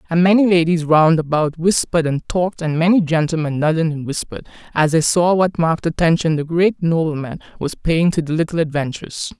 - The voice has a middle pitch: Yes, medium, 165 Hz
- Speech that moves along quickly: No, average, 185 wpm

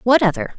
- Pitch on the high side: Yes, high, 215 Hz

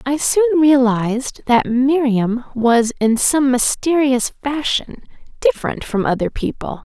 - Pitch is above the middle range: Yes, very high, 260 Hz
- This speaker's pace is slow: Yes, slow, 120 wpm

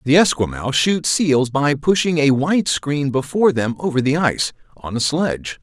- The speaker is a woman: No, male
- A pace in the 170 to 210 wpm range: Yes, average, 180 wpm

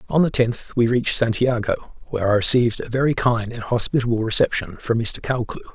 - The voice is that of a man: Yes, male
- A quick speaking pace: No, average, 190 wpm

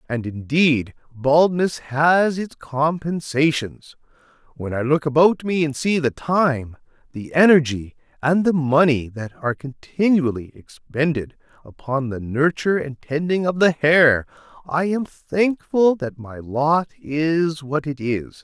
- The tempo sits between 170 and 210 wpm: No, slow, 135 wpm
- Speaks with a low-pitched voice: No, medium, 150 Hz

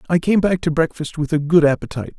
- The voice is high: No, medium, 160 Hz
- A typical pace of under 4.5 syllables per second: No, 6.8 syllables/s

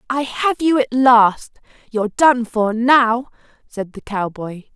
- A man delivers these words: No, female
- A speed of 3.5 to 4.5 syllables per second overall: Yes, 3.8 syllables/s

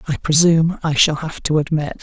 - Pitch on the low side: No, medium, 155 Hz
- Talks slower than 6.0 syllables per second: Yes, 5.5 syllables/s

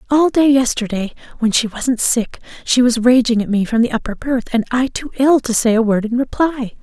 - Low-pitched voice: No, high, 240 Hz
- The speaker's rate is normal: No, fast, 230 wpm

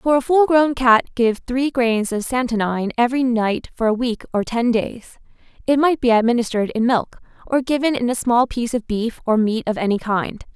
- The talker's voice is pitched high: Yes, high, 240 Hz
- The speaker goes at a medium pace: No, fast, 210 wpm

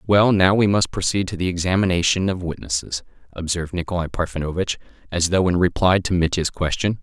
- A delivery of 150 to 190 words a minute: Yes, average, 170 wpm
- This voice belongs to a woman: No, male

